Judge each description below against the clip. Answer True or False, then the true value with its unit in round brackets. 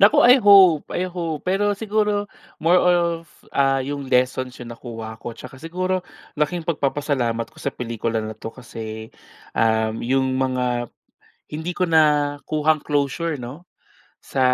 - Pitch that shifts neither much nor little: False (5.7 semitones)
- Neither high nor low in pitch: True (145 Hz)